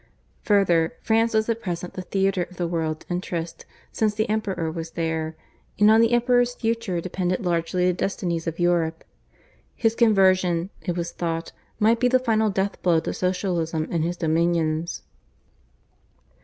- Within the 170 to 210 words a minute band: No, average, 155 wpm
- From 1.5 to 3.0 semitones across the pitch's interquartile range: No, average, 4.4 semitones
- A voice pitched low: No, medium, 180 Hz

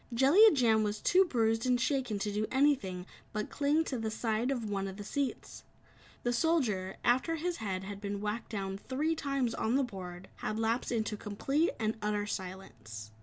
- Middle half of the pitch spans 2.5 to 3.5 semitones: No, average, 4.7 semitones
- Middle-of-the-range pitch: No, high, 220 Hz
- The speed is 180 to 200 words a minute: Yes, average, 185 wpm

